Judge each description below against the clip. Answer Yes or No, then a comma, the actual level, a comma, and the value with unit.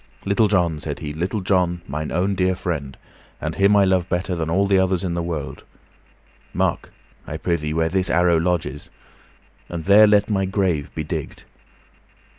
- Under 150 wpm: No, average, 170 wpm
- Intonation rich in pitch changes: No, average, 3.0 semitones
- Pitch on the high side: No, very low, 90 Hz